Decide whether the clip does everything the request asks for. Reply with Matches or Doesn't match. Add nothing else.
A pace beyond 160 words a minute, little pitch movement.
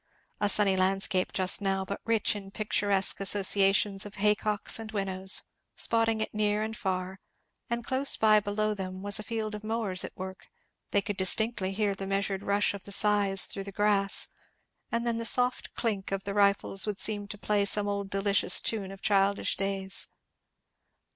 Matches